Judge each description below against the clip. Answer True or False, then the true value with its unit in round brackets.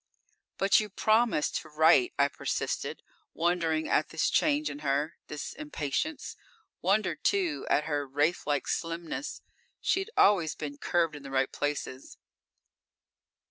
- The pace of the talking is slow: True (130 wpm)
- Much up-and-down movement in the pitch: True (6.6 semitones)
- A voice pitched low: False (165 Hz)